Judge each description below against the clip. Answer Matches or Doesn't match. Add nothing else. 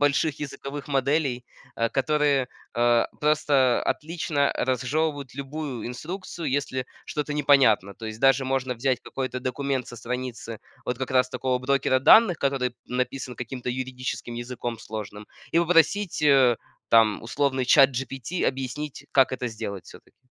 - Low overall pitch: Matches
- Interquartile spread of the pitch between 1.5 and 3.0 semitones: Matches